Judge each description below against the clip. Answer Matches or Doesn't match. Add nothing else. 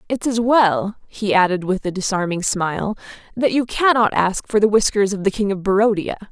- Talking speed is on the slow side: Doesn't match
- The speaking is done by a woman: Matches